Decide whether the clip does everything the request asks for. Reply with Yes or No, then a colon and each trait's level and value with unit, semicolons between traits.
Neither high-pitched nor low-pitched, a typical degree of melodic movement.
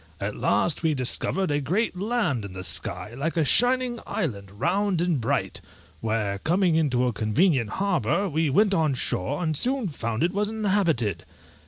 No: medium, 160 Hz; wide, 8.9 semitones